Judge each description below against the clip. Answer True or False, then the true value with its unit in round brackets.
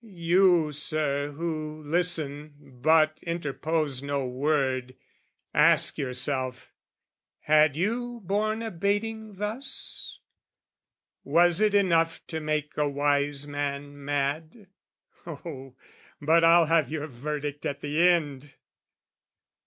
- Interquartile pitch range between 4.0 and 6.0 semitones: False (3.2 semitones)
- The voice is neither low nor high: True (155 Hz)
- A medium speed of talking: False (105 wpm)